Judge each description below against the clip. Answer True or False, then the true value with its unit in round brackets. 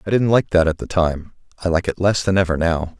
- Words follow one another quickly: True (280 wpm)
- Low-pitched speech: True (90 Hz)